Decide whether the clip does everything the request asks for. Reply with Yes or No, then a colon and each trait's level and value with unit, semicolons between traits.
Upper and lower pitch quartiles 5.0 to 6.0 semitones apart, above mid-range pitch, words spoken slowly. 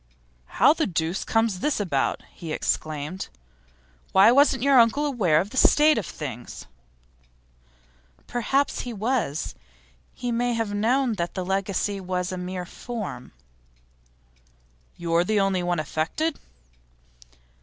Yes: wide, 5.6 semitones; high, 200 Hz; slow, 130 wpm